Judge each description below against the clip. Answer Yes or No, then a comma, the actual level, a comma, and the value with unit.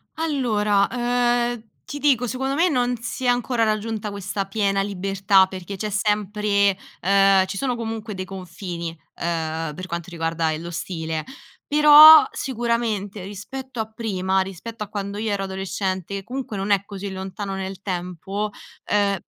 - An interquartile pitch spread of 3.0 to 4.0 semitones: Yes, average, 3.4 semitones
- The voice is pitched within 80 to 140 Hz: No, high, 200 Hz